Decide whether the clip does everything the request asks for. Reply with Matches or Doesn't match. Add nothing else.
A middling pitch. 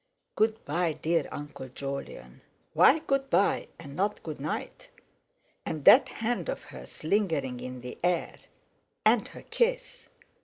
Matches